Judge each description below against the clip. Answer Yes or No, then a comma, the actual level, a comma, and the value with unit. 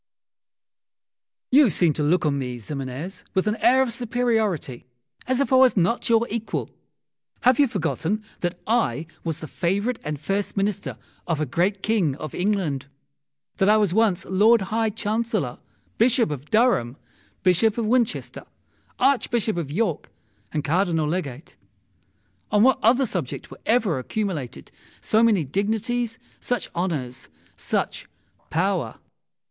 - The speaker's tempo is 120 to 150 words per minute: Yes, average, 140 wpm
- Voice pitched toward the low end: No, high, 195 Hz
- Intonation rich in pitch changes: Yes, wide, 6.5 semitones